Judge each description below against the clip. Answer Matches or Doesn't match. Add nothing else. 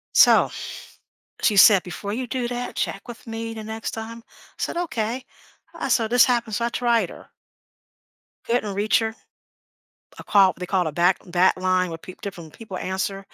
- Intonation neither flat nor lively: Matches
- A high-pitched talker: Matches